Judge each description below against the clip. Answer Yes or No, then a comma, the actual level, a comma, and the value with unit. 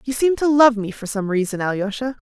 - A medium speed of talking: No, fast, 235 wpm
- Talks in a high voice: Yes, high, 230 Hz